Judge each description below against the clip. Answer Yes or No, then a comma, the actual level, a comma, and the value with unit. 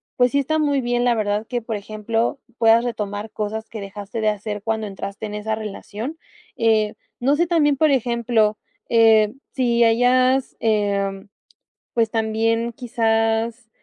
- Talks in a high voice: Yes, high, 225 Hz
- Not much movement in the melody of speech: Yes, narrow, 2.3 semitones